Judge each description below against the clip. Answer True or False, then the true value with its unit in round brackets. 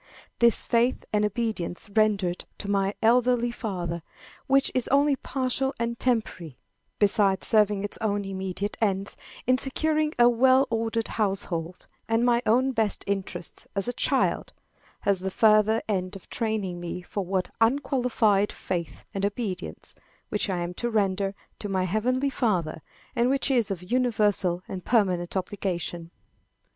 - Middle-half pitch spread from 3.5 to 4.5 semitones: True (4.0 semitones)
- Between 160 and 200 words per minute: False (145 wpm)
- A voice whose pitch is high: True (210 Hz)